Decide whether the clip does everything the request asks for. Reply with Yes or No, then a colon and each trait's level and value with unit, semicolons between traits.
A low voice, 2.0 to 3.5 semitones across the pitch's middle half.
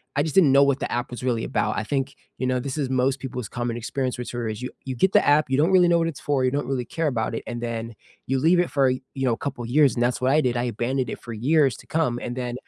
Yes: low, 130 Hz; average, 2.8 semitones